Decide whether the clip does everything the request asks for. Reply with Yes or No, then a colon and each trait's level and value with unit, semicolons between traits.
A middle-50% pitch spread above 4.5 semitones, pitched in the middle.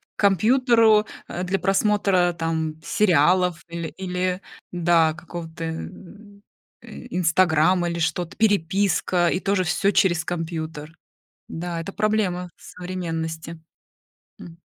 No: average, 2.8 semitones; medium, 175 Hz